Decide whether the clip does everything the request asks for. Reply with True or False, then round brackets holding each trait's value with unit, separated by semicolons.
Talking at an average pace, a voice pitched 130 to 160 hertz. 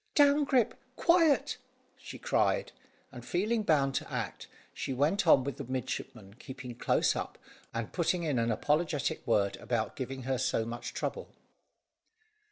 True (150 wpm; 140 Hz)